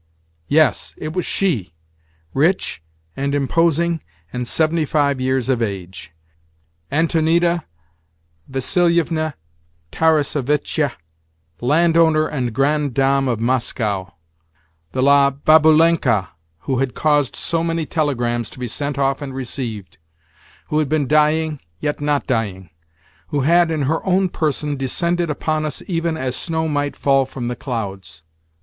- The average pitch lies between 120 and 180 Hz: Yes, medium, 140 Hz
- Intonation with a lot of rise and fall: Yes, wide, 5.8 semitones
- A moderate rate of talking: No, slow, 120 wpm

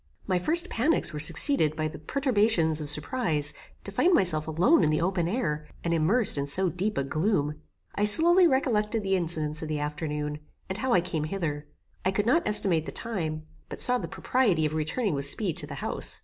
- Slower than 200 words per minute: No, fast, 205 wpm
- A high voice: No, medium, 170 Hz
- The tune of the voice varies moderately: No, wide, 6.1 semitones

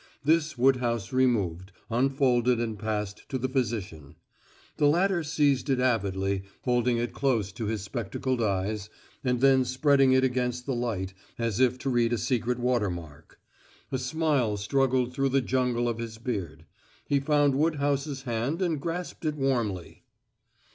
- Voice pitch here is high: No, low, 125 Hz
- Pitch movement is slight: No, average, 3.6 semitones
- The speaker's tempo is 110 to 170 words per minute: Yes, average, 155 wpm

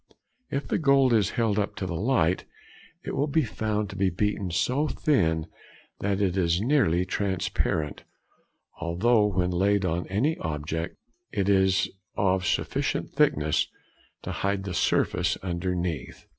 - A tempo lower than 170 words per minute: Yes, average, 145 wpm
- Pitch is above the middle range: No, very low, 95 Hz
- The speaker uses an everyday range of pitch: Yes, average, 3.5 semitones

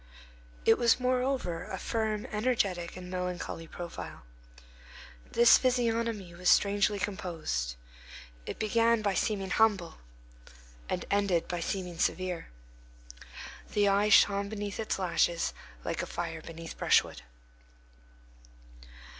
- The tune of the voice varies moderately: Yes, average, 3.8 semitones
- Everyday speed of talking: No, slow, 110 wpm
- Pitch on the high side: Yes, high, 200 Hz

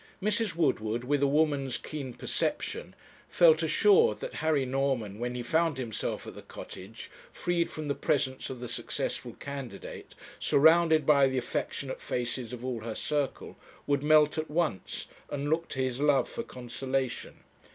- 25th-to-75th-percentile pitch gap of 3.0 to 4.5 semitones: Yes, average, 3.9 semitones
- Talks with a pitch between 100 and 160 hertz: Yes, medium, 140 Hz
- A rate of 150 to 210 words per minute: Yes, average, 160 wpm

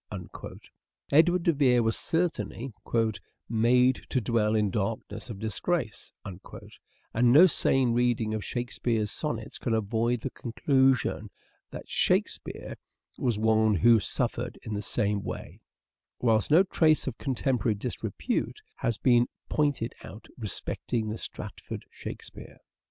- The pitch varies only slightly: No, average, 3.3 semitones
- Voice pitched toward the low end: Yes, low, 115 Hz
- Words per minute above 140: No, slow, 135 wpm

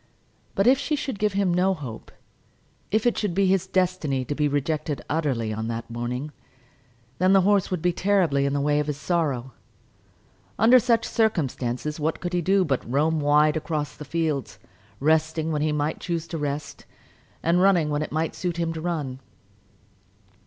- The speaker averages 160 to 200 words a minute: Yes, average, 185 wpm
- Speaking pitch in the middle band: Yes, medium, 155 Hz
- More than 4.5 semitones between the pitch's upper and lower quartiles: No, average, 4.2 semitones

